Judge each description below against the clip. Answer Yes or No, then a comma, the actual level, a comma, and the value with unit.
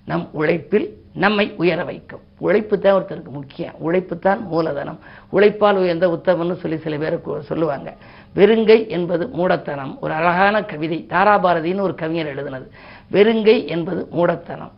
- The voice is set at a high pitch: No, medium, 175 Hz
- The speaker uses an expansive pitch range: No, average, 3.3 semitones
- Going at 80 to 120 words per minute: No, fast, 130 wpm